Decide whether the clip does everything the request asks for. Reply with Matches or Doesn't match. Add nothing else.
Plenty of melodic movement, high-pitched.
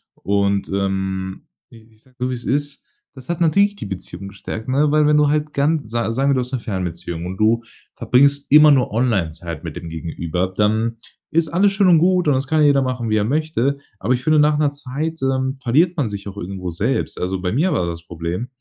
Doesn't match